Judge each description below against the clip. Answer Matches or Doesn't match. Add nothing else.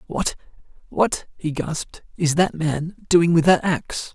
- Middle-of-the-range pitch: Matches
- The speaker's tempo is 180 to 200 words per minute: Doesn't match